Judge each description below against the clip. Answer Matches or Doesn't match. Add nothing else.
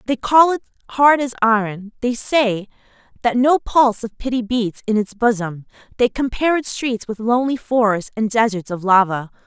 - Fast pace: Doesn't match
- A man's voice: Doesn't match